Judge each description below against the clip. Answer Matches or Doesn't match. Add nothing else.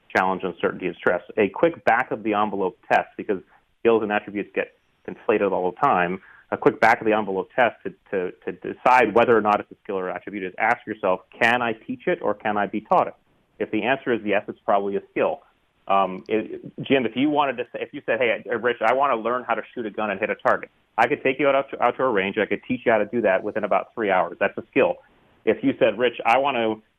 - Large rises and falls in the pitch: Doesn't match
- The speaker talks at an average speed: Doesn't match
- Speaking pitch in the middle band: Doesn't match